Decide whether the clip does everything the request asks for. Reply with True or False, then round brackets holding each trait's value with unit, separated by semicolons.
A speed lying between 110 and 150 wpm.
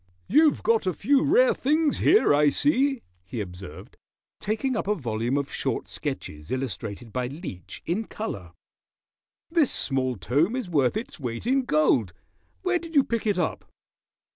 False (160 wpm)